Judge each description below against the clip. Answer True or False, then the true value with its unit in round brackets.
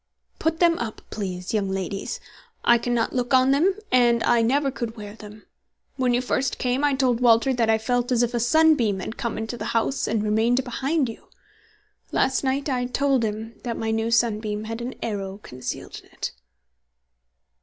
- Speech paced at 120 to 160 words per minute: False (185 wpm)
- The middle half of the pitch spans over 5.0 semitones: False (2.9 semitones)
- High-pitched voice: True (235 Hz)